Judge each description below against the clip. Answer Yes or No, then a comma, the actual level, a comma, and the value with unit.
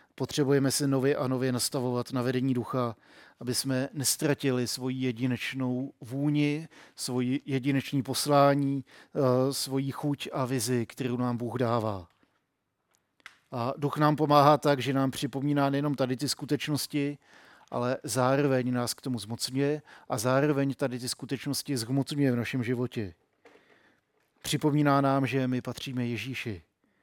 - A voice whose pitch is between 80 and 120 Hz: No, low, 135 Hz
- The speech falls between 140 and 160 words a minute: No, average, 130 wpm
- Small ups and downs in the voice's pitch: Yes, narrow, 2.0 semitones